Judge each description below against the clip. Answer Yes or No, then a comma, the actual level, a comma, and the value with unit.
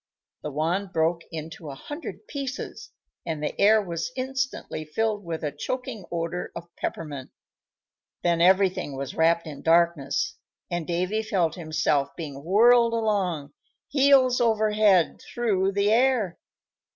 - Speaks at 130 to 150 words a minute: Yes, slow, 135 wpm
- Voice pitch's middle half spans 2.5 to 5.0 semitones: No, wide, 5.4 semitones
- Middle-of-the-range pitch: Yes, medium, 180 Hz